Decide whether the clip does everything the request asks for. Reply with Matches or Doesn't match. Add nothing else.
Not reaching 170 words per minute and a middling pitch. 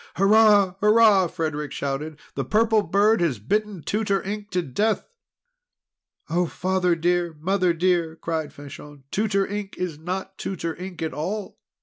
Matches